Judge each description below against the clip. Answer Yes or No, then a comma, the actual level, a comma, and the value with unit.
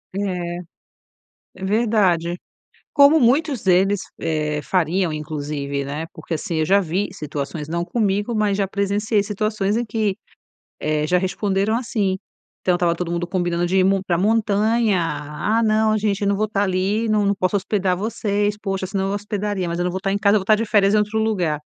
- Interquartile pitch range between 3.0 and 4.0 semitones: Yes, average, 3.3 semitones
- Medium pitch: No, high, 195 Hz